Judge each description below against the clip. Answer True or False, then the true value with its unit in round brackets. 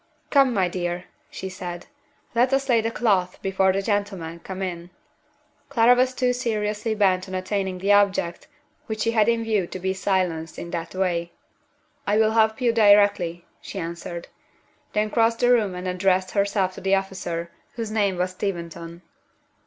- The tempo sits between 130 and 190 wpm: True (170 wpm)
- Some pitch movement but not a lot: True (3.3 semitones)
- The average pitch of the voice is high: True (195 Hz)